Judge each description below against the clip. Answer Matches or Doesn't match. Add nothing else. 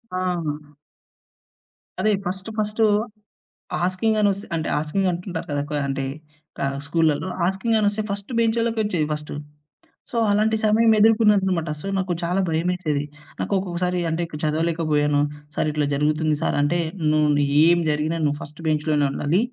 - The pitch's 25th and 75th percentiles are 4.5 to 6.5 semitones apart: Matches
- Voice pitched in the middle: Matches